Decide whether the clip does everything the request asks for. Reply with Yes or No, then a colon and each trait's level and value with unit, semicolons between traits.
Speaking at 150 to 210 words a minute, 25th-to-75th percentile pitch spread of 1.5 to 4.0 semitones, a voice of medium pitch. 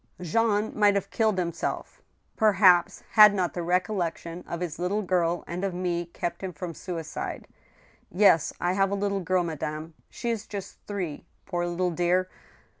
Yes: average, 175 wpm; narrow, 2.6 semitones; medium, 180 Hz